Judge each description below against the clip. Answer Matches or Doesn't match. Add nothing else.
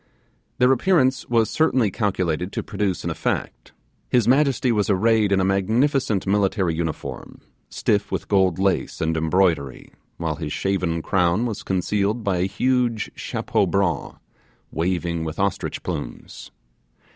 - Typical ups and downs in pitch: Matches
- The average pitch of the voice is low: Matches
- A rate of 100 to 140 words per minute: Matches